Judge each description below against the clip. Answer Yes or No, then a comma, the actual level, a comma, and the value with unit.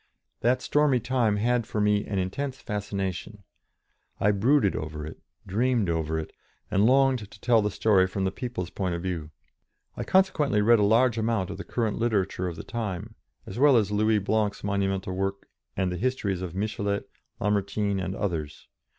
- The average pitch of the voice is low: Yes, low, 105 Hz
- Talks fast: No, average, 175 wpm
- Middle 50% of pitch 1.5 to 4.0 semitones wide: Yes, average, 3.6 semitones